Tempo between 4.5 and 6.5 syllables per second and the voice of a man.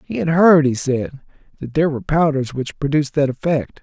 Yes: 5.6 syllables/s; male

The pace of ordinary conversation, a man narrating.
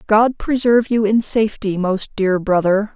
No: average, 160 wpm; female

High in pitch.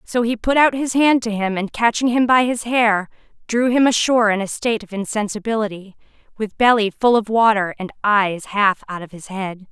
Yes: high, 220 Hz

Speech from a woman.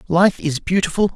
No: male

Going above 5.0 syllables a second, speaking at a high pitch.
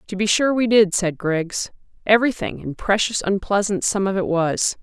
No: 4.9 syllables/s; high, 200 Hz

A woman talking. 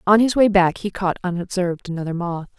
Yes: female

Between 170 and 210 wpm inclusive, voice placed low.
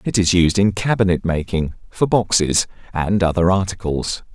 No: average, 150 wpm; very low, 90 Hz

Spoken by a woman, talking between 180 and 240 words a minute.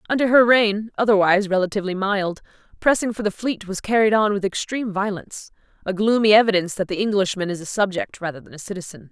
Yes: female; average, 185 wpm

